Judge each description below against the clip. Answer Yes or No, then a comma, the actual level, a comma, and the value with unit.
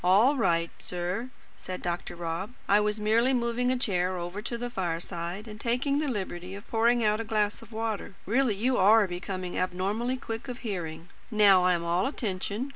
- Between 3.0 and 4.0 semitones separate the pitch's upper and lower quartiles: No, average, 4.5 semitones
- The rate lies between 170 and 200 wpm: Yes, average, 190 wpm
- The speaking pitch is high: Yes, high, 210 Hz